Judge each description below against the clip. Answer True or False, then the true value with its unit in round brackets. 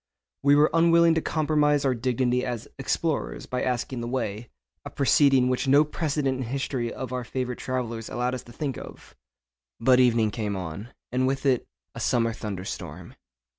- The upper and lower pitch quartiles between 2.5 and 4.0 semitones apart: True (2.9 semitones)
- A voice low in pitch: True (125 Hz)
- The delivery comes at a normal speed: True (175 wpm)